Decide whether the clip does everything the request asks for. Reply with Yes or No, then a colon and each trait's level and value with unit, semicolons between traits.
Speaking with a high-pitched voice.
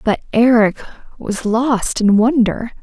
Yes: high, 230 Hz